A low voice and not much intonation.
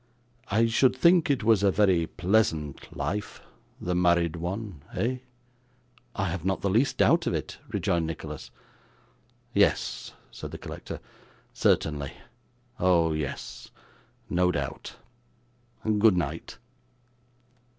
No: very low, 90 Hz; average, 4.5 semitones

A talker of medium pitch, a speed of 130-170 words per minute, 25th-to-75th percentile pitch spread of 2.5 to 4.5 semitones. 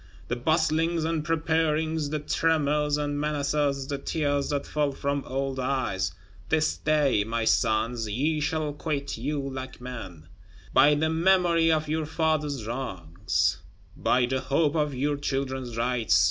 Yes: medium, 145 Hz; average, 145 wpm; average, 3.2 semitones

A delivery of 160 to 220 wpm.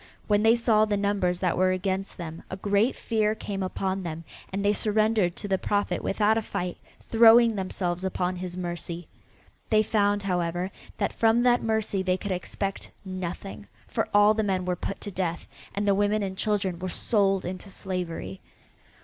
Yes: average, 180 wpm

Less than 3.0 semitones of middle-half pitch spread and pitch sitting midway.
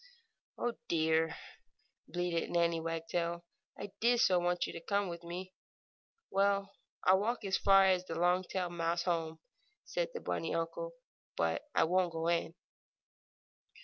Yes: narrow, 2.5 semitones; medium, 175 Hz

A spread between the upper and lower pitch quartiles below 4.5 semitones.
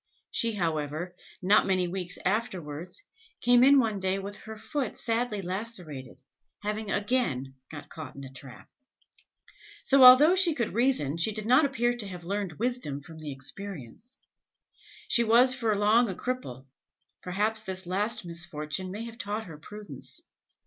No: wide, 5.6 semitones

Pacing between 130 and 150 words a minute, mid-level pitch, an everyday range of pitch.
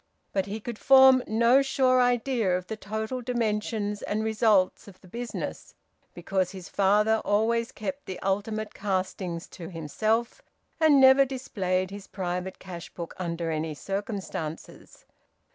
No: average, 140 wpm; high, 210 Hz; average, 4.2 semitones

